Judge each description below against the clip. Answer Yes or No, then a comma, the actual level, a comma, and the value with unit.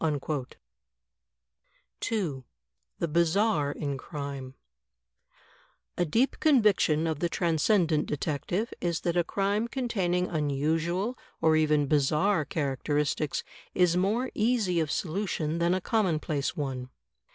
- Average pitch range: Yes, average, 4.7 semitones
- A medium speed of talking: No, slow, 105 wpm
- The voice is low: No, medium, 165 Hz